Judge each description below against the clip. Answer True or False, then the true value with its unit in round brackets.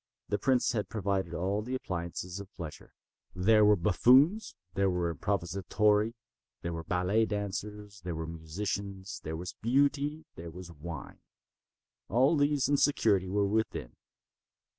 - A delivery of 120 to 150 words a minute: True (140 wpm)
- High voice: False (100 Hz)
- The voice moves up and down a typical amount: True (4.0 semitones)